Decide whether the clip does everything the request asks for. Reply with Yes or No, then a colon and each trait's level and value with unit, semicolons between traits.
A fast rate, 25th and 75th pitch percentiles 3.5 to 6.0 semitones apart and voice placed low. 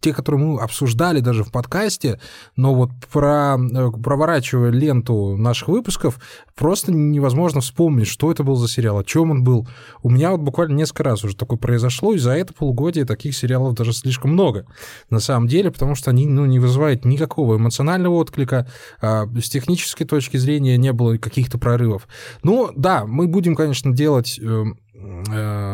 Yes: fast, 170 wpm; average, 4.0 semitones; low, 130 Hz